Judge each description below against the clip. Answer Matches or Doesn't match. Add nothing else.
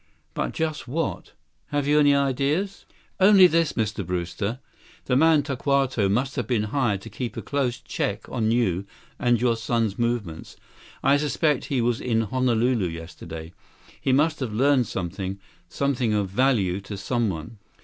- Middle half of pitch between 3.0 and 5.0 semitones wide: Doesn't match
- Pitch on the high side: Doesn't match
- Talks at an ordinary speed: Matches